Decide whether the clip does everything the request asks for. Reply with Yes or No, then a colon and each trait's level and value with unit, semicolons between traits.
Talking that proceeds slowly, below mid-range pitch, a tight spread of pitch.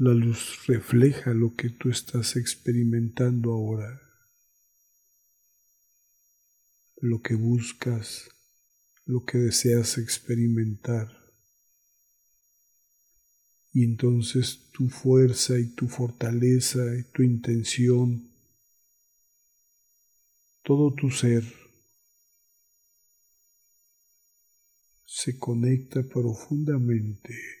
Yes: slow, 70 wpm; low, 120 Hz; narrow, 1.5 semitones